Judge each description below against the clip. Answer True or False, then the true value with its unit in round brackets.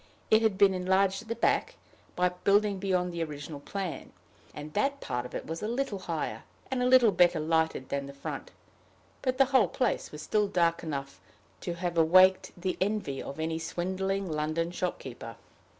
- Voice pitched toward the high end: False (180 Hz)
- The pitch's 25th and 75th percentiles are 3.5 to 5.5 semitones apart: True (4.0 semitones)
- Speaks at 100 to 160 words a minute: False (180 wpm)